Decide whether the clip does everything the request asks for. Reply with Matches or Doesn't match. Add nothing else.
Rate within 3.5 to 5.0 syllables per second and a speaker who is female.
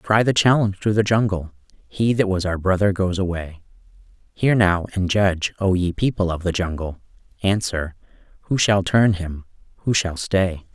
Doesn't match